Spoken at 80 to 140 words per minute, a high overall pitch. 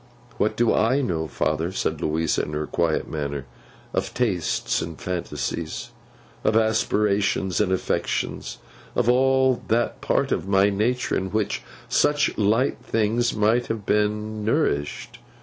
No: slow, 135 wpm; low, 105 Hz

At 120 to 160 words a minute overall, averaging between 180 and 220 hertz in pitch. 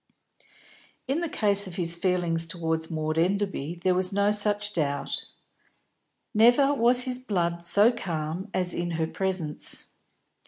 Yes: slow, 135 wpm; medium, 185 Hz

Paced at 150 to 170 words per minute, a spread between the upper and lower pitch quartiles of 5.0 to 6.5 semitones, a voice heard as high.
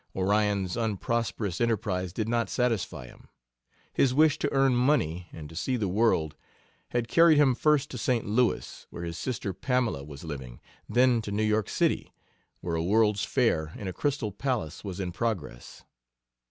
No: average, 165 wpm; wide, 5.5 semitones; low, 105 Hz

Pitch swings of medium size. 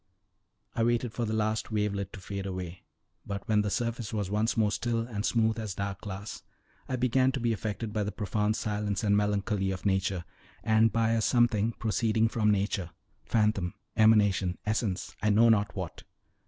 No: narrow, 2.1 semitones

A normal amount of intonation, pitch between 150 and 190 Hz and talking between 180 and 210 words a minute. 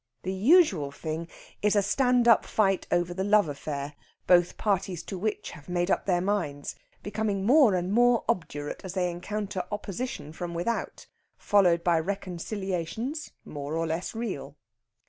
No: average, 3.8 semitones; medium, 185 Hz; average, 155 wpm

